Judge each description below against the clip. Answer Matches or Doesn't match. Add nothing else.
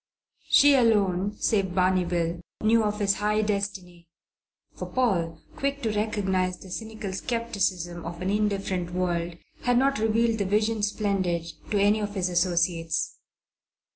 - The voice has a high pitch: Matches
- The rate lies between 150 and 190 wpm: Doesn't match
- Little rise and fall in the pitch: Doesn't match